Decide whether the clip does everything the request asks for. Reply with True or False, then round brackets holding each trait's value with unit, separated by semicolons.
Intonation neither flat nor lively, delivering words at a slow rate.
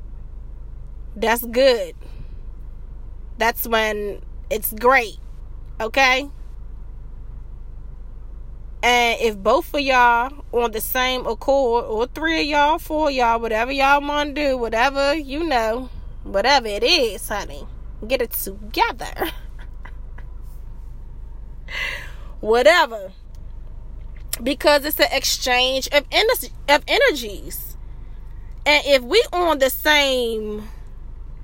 True (4.4 semitones; 105 wpm)